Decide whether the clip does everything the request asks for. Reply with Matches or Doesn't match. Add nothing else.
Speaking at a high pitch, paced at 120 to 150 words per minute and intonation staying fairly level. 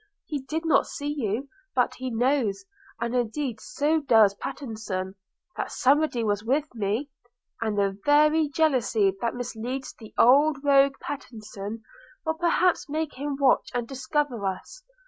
Doesn't match